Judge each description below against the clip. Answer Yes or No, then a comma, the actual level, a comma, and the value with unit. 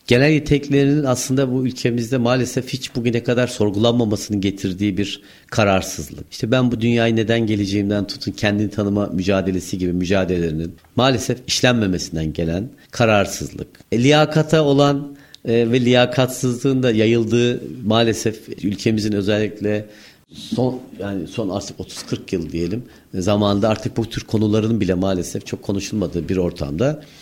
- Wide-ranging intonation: No, average, 4.0 semitones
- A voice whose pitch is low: Yes, low, 110 Hz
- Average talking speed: Yes, average, 125 wpm